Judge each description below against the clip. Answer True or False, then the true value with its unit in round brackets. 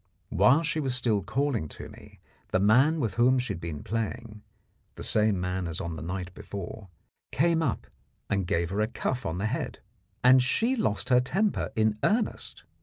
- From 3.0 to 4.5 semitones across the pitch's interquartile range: False (5.6 semitones)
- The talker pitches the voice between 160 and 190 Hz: False (110 Hz)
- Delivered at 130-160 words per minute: False (185 wpm)